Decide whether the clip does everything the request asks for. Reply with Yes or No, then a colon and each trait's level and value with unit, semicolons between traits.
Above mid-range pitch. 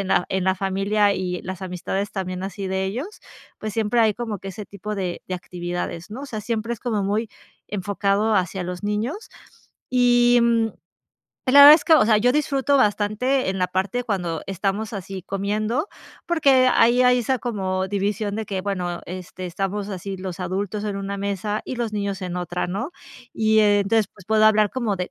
Yes: high, 205 Hz